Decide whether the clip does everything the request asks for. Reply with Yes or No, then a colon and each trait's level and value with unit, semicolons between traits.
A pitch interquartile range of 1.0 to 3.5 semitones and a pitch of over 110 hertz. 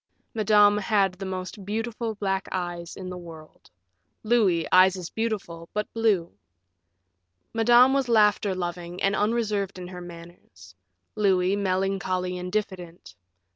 Yes: average, 2.9 semitones; high, 190 Hz